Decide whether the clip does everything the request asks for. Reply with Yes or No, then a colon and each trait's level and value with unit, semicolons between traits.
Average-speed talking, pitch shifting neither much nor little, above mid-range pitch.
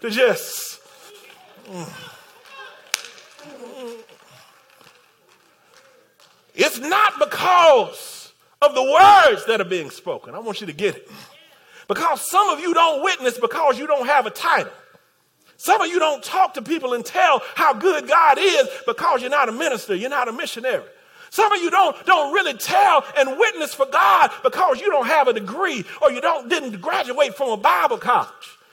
No: average, 165 wpm; wide, 6.9 semitones; very high, 325 Hz